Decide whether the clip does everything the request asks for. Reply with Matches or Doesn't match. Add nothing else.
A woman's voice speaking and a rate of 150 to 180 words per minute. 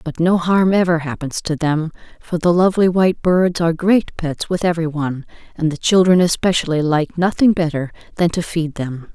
Doesn't match